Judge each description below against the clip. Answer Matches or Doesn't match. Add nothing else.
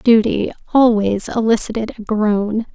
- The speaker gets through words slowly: Matches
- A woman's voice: Matches